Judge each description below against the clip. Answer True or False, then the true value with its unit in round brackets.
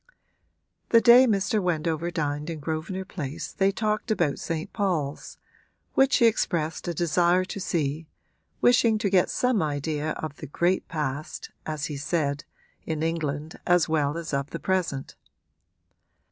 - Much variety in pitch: False (4.0 semitones)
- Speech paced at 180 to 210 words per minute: False (145 wpm)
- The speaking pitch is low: False (165 Hz)